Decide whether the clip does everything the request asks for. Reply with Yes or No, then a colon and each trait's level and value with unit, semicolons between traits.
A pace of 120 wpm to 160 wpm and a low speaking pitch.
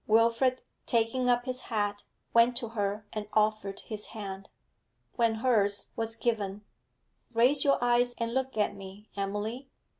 No: average, 145 wpm; high, 225 Hz